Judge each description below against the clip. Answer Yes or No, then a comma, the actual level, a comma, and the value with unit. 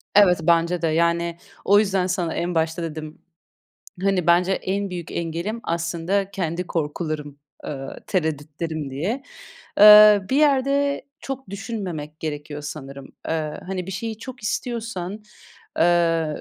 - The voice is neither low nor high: Yes, medium, 175 Hz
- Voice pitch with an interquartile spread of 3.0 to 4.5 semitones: Yes, average, 4.1 semitones